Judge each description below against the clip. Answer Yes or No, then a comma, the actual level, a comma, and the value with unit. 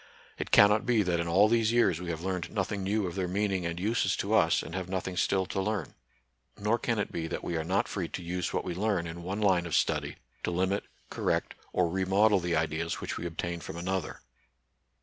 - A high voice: No, very low, 95 Hz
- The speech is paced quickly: Yes, fast, 230 wpm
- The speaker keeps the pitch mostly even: No, average, 3.0 semitones